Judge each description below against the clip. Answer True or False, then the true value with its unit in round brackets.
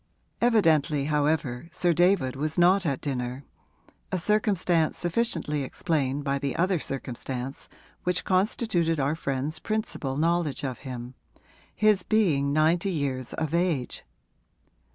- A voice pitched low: False (155 Hz)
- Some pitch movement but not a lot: True (4.5 semitones)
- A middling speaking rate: False (120 wpm)